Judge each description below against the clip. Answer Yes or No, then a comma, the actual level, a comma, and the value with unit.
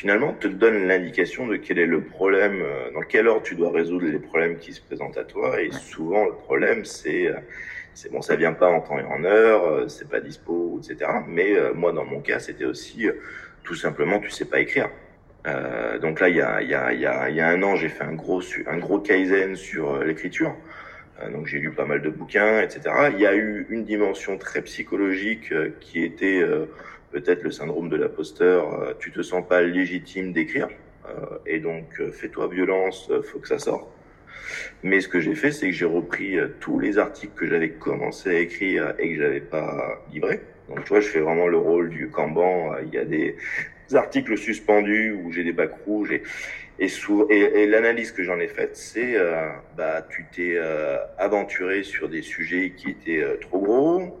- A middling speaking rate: Yes, average, 210 wpm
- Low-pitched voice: No, very high, 375 Hz